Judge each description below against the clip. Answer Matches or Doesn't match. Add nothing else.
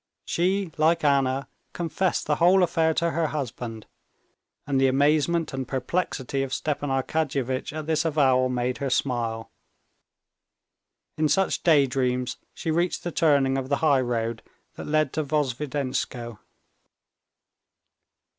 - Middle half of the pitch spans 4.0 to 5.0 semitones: Doesn't match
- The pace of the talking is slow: Matches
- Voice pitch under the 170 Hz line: Matches